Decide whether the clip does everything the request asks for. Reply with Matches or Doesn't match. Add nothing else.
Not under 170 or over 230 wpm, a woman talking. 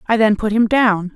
Doesn't match